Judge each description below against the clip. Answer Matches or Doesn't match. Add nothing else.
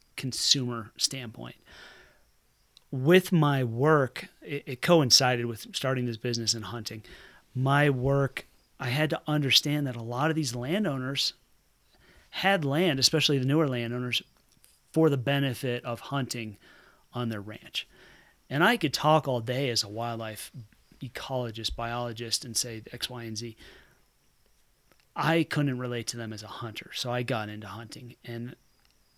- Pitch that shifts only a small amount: Doesn't match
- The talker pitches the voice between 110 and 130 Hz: Matches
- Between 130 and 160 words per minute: Matches